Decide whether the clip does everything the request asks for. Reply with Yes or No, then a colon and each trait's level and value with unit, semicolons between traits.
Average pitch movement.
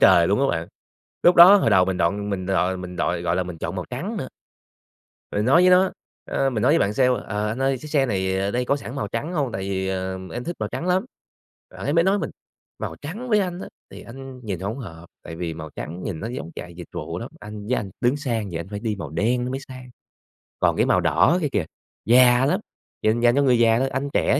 No: wide, 6.3 semitones